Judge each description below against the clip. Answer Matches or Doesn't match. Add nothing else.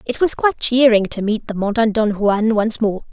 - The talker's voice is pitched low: Doesn't match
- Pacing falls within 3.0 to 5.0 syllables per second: Doesn't match